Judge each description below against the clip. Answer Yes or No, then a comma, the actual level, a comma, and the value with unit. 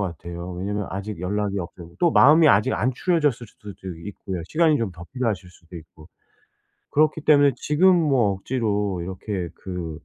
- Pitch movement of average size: No, wide, 7.4 semitones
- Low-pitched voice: Yes, low, 100 Hz